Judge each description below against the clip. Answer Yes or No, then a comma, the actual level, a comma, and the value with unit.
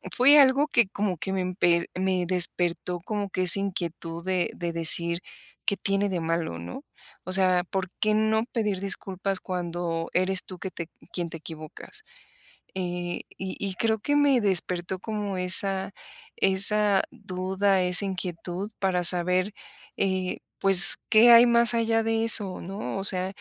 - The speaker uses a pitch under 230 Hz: Yes, high, 190 Hz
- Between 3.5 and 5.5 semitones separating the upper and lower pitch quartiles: No, narrow, 2.5 semitones